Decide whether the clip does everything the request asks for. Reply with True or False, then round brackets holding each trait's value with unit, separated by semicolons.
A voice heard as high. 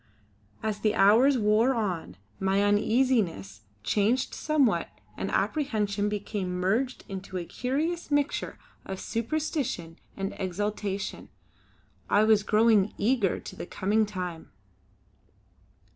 True (210 Hz)